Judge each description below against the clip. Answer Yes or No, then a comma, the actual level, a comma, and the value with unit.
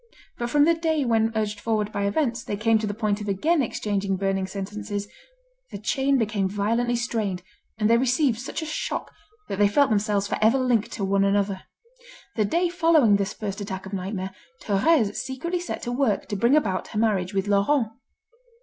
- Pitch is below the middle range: No, high, 215 Hz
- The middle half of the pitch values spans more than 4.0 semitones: No, average, 3.7 semitones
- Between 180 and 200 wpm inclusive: Yes, average, 195 wpm